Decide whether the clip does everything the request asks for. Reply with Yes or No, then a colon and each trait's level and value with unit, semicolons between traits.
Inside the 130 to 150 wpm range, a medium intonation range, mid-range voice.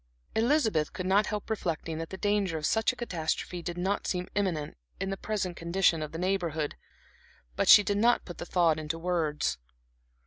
No: average, 185 wpm; average, 3.9 semitones; medium, 180 Hz